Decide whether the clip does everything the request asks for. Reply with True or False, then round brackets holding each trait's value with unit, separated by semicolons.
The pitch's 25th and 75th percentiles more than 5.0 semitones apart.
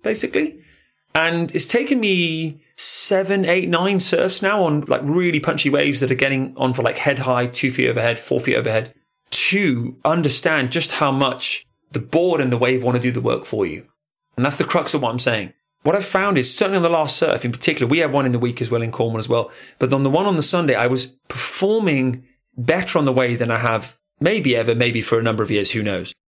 True (5.5 semitones)